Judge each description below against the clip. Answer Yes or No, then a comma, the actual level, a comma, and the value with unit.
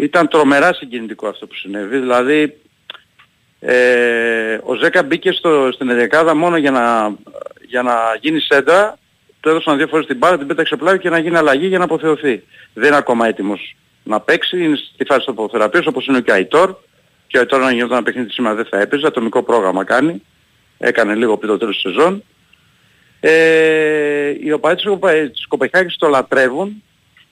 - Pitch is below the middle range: No, medium, 150 Hz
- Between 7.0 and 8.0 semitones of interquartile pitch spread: No, average, 5.1 semitones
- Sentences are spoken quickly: Yes, fast, 180 wpm